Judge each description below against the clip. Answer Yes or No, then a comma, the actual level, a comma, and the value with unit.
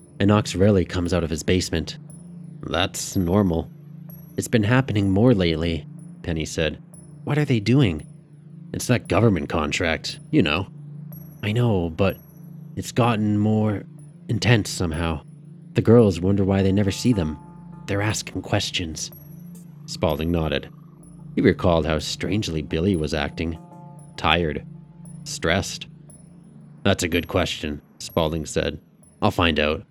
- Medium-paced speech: No, slow, 130 wpm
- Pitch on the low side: Yes, low, 110 Hz